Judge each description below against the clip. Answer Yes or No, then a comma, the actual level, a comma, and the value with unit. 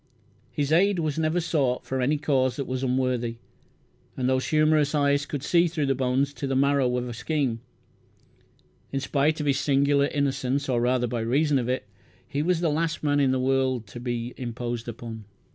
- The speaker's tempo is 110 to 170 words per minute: No, average, 195 wpm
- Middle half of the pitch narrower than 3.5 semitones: Yes, average, 2.8 semitones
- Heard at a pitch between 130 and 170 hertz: Yes, low, 135 Hz